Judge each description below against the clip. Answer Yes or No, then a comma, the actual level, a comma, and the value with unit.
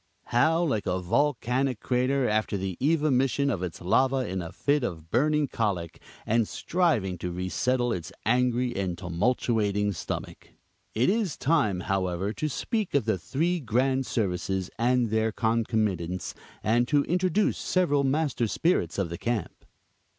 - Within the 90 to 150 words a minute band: Yes, average, 145 wpm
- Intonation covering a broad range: Yes, wide, 6.2 semitones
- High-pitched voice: No, low, 120 Hz